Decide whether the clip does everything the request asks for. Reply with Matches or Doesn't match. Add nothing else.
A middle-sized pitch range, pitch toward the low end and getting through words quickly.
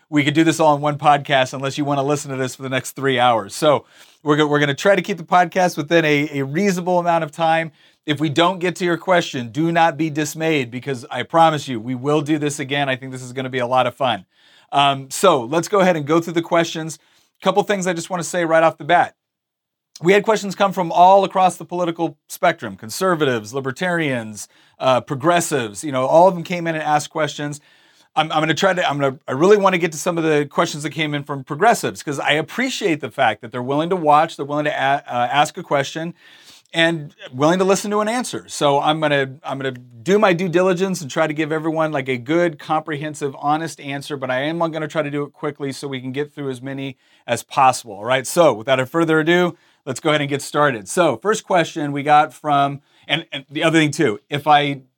Doesn't match